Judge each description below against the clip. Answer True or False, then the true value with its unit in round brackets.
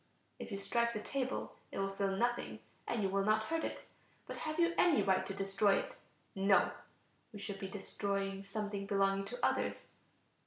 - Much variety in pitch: False (3.1 semitones)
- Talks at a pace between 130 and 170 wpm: False (185 wpm)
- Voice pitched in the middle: False (200 Hz)